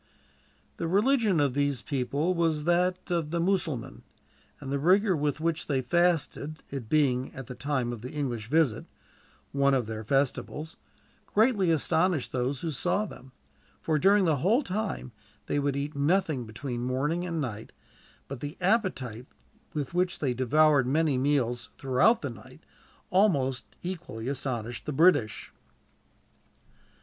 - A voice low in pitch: No, medium, 145 Hz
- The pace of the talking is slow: No, average, 145 wpm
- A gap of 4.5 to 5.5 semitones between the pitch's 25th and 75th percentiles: Yes, average, 5.1 semitones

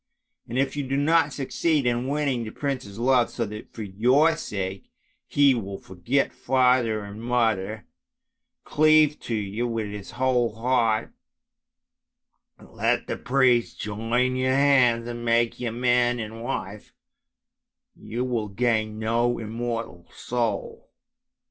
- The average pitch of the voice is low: Yes, low, 120 Hz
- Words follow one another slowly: Yes, slow, 130 wpm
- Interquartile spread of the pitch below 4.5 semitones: Yes, average, 2.9 semitones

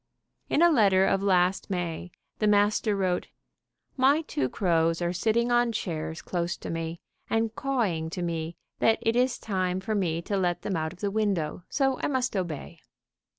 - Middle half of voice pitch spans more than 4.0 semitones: Yes, average, 4.7 semitones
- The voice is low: No, high, 190 Hz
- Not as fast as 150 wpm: No, average, 180 wpm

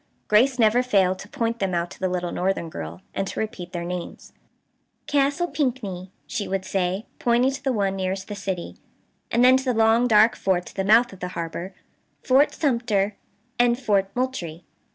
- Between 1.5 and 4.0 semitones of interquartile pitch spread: No, average, 4.8 semitones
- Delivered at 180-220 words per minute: Yes, average, 190 wpm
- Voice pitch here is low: No, high, 205 Hz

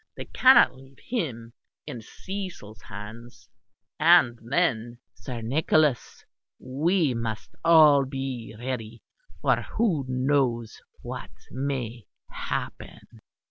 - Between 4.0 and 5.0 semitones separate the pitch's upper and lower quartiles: Yes, average, 4.5 semitones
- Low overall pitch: Yes, low, 130 Hz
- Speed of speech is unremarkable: No, slow, 100 wpm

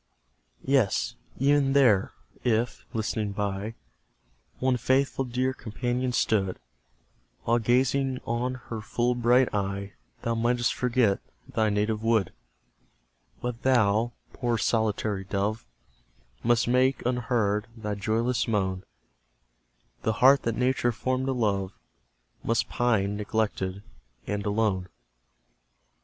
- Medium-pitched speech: No, low, 115 Hz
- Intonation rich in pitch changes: No, average, 3.3 semitones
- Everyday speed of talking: No, slow, 110 wpm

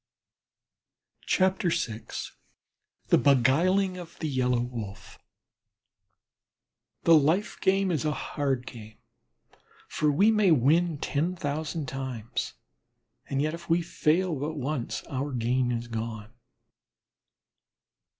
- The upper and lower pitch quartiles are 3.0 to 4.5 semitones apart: No, wide, 5.4 semitones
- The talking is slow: Yes, slow, 100 wpm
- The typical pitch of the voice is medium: Yes, medium, 145 Hz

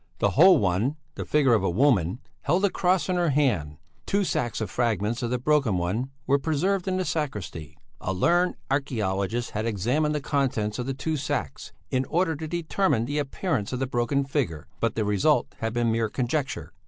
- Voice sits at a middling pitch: No, low, 130 Hz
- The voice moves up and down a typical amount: No, wide, 5.9 semitones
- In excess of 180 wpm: Yes, average, 195 wpm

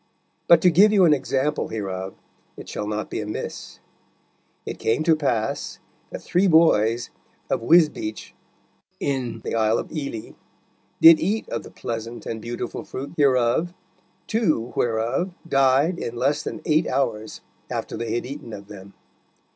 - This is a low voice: Yes, low, 130 Hz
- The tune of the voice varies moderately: No, wide, 6.0 semitones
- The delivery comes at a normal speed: Yes, average, 150 wpm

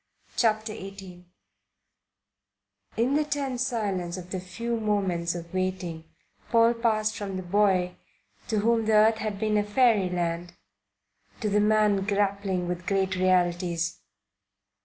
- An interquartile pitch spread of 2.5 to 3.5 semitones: Yes, average, 3.2 semitones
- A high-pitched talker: Yes, high, 200 Hz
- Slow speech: Yes, slow, 130 wpm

